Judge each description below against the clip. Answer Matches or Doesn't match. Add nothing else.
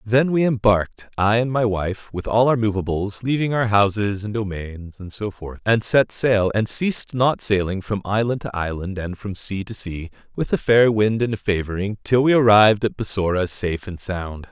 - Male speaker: Matches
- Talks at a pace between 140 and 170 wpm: Doesn't match